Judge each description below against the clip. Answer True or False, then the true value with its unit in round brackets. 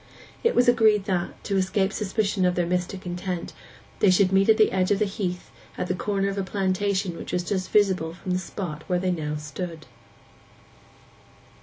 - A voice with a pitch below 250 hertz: True (190 Hz)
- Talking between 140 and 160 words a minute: False (185 wpm)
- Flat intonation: True (2.0 semitones)